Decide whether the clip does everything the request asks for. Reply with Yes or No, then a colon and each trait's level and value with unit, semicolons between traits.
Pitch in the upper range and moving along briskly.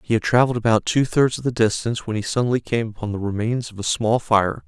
No: low, 115 Hz; fast, 255 wpm